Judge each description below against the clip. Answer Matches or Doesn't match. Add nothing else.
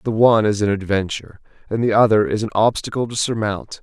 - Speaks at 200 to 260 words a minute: Matches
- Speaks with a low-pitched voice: Matches